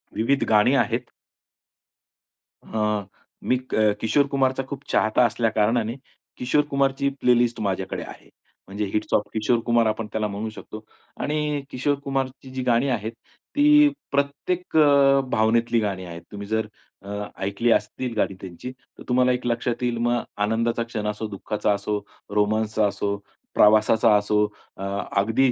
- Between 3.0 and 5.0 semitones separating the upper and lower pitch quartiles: Yes, average, 3.6 semitones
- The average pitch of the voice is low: Yes, low, 115 Hz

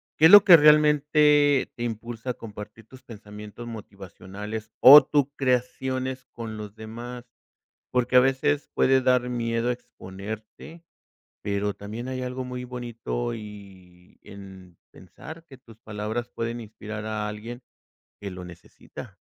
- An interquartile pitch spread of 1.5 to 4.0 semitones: Yes, average, 3.6 semitones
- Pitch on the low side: Yes, low, 115 Hz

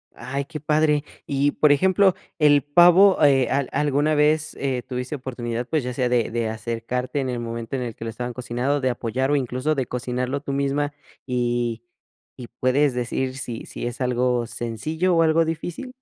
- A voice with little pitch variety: No, average, 3.4 semitones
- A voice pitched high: No, low, 130 Hz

